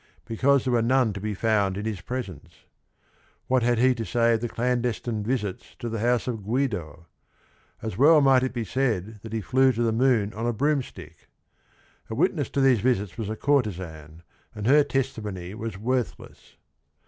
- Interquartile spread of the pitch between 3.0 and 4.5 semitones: Yes, average, 3.7 semitones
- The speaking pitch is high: No, low, 115 Hz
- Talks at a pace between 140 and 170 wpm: No, average, 185 wpm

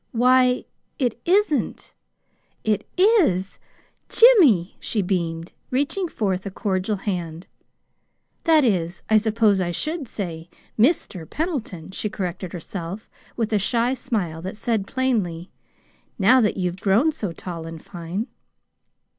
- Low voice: No, high, 205 Hz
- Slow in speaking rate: Yes, slow, 125 wpm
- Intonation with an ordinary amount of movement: No, wide, 6.0 semitones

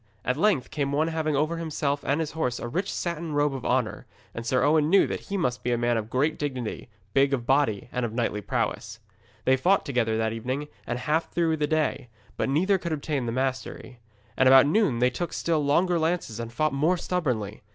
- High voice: No, medium, 140 Hz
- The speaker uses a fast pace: Yes, fast, 220 wpm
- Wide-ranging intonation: No, average, 4.4 semitones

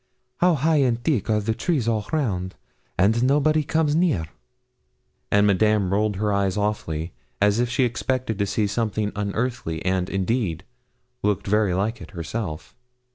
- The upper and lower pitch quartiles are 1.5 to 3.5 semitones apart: No, average, 4.1 semitones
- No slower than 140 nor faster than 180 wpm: Yes, average, 155 wpm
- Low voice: Yes, low, 105 Hz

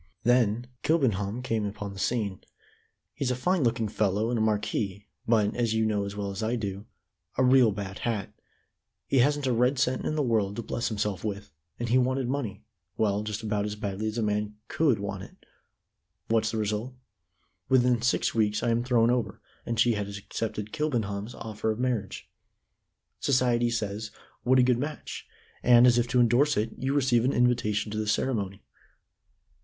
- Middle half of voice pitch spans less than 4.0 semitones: Yes, average, 3.0 semitones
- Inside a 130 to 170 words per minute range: No, average, 185 wpm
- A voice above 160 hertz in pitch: No, low, 115 Hz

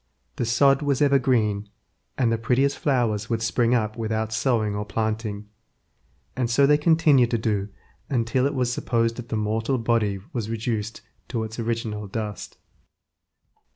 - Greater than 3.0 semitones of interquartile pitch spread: No, average, 2.7 semitones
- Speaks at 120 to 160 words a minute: Yes, average, 155 wpm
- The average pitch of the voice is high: No, low, 115 Hz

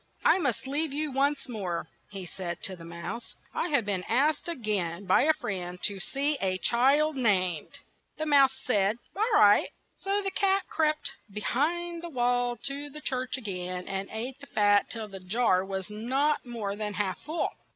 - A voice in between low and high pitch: No, high, 240 Hz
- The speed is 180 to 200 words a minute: Yes, average, 190 wpm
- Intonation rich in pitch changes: Yes, wide, 6.9 semitones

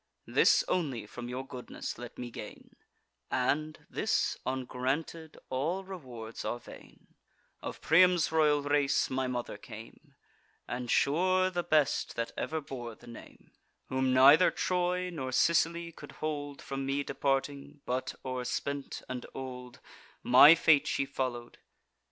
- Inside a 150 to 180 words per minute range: No, slow, 135 wpm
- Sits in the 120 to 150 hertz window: Yes, medium, 140 Hz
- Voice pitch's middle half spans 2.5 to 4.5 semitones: Yes, average, 3.8 semitones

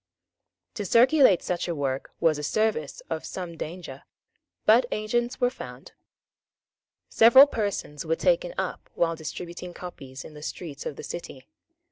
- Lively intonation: Yes, wide, 6.6 semitones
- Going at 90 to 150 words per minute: Yes, average, 145 wpm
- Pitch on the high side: No, medium, 175 Hz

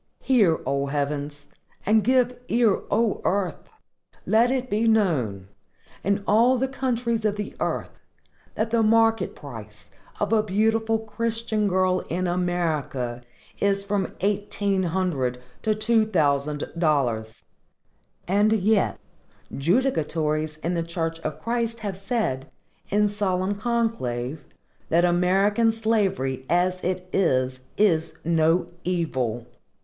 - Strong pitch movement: Yes, wide, 5.9 semitones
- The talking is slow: Yes, slow, 120 wpm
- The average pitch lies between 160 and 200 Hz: Yes, high, 190 Hz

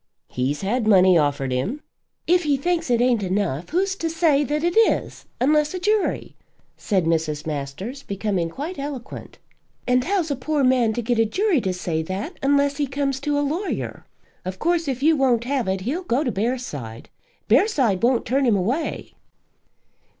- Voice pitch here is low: No, very high, 255 Hz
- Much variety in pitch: Yes, wide, 7.8 semitones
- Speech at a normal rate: Yes, average, 180 wpm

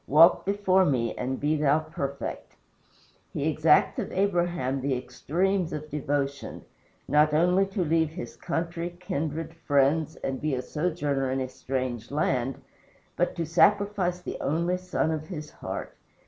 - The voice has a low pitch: No, medium, 155 Hz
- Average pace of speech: Yes, average, 145 wpm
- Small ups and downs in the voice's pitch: No, average, 4.1 semitones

